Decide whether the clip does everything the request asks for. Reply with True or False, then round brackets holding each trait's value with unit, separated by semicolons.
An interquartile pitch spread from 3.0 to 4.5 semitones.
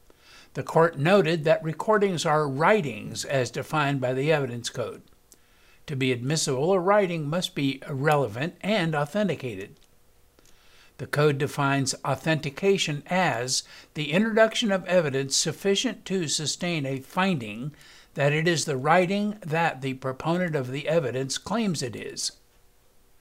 False (5.0 semitones)